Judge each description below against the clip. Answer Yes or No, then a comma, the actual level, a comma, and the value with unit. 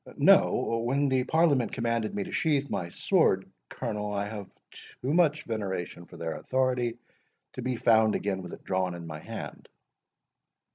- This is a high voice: No, low, 115 Hz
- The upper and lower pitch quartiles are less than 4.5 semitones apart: No, average, 5.1 semitones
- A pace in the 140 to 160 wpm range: Yes, average, 155 wpm